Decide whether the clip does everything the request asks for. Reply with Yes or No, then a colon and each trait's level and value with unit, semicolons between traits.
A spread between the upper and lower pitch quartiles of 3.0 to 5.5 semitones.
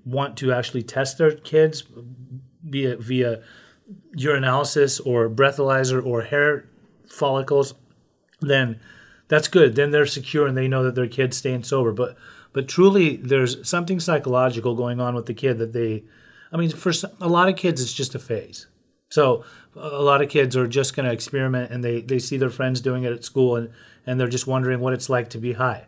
No: narrow, 2.6 semitones